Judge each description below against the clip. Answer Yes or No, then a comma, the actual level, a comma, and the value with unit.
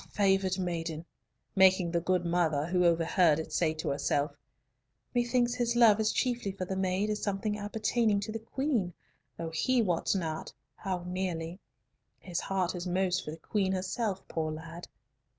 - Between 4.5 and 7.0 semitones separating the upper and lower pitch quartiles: No, average, 3.6 semitones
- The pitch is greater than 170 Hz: Yes, medium, 185 Hz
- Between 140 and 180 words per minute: Yes, average, 165 wpm